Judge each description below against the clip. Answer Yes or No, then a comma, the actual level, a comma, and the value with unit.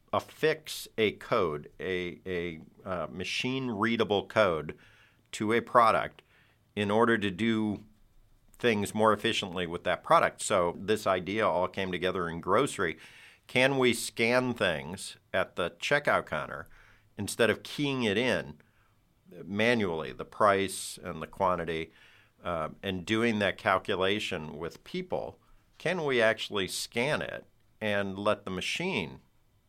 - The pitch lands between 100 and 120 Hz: Yes, low, 105 Hz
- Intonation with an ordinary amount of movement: Yes, average, 3.5 semitones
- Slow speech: Yes, slow, 130 wpm